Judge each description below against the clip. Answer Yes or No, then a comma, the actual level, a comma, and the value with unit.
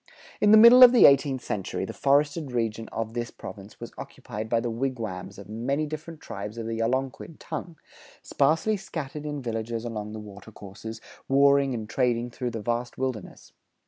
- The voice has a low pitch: Yes, low, 120 Hz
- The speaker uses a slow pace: No, average, 175 wpm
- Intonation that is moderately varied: Yes, average, 4.1 semitones